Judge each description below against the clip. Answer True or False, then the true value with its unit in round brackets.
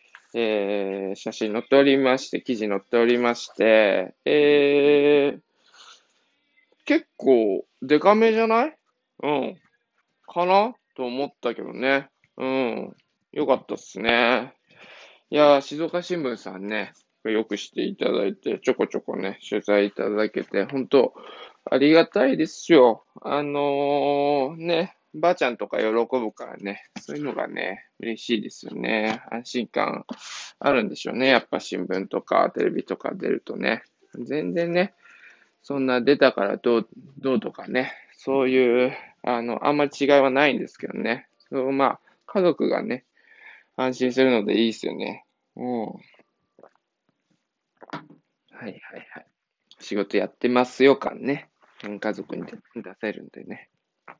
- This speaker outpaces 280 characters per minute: False (260 characters per minute)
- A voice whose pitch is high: False (130 Hz)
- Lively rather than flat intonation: False (4.3 semitones)